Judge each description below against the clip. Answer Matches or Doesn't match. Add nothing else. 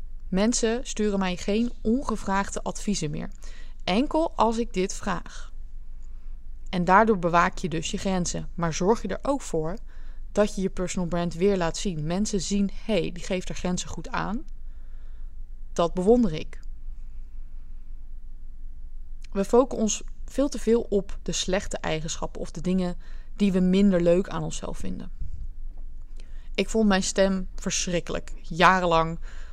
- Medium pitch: Matches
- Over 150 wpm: Doesn't match